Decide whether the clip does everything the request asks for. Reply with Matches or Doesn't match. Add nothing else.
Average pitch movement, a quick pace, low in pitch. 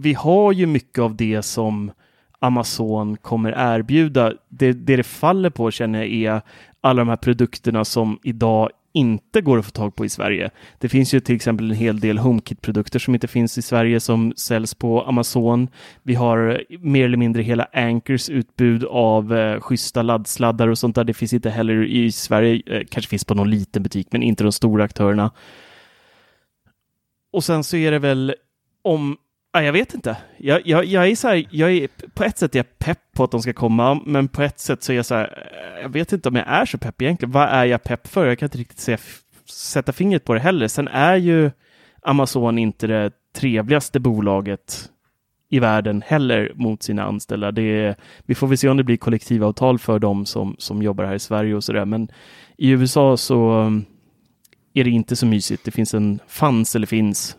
Matches